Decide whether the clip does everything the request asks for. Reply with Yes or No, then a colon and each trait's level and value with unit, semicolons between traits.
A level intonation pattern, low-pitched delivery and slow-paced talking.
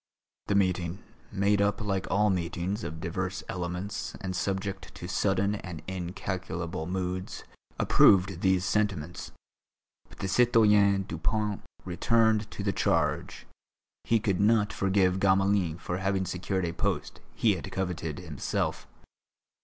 Yes: narrow, 2.2 semitones; very low, 95 Hz; slow, 130 wpm